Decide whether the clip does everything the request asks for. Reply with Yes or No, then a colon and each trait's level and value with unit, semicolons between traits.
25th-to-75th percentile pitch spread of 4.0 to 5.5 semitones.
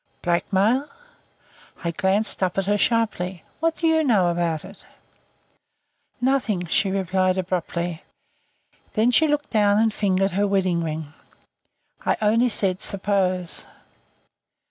No: average, 3.5 semitones